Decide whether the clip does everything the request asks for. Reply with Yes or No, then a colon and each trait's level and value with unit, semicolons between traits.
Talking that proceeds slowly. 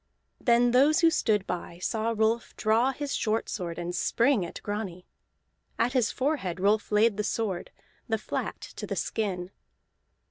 No: average, 155 wpm